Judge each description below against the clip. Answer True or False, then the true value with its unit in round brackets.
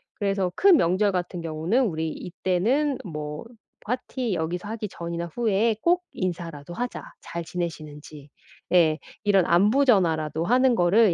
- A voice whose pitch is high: False (180 Hz)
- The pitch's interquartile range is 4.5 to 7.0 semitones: True (5.2 semitones)